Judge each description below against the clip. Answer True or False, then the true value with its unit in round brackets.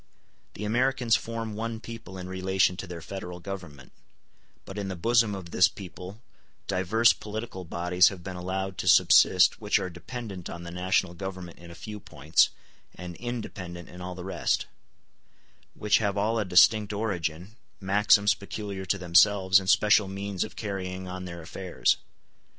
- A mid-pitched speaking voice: False (95 Hz)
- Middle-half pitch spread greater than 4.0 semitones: False (2.8 semitones)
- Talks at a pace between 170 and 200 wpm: False (160 wpm)